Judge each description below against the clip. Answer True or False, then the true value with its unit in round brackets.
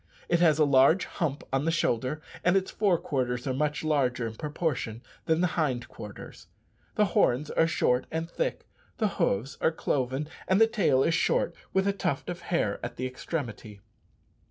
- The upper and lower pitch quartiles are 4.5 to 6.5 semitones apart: True (5.0 semitones)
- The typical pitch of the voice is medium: True (150 Hz)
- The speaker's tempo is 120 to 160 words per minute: False (180 wpm)